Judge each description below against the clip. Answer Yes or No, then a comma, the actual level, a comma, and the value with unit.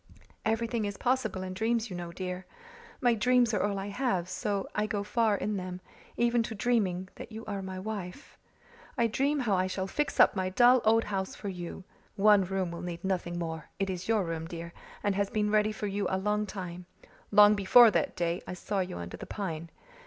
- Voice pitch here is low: No, high, 200 Hz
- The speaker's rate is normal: No, fast, 210 wpm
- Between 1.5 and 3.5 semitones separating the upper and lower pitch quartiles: Yes, average, 3.1 semitones